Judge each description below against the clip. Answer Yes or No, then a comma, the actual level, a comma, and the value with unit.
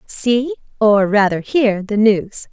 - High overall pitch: Yes, high, 210 Hz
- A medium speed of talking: Yes, average, 145 wpm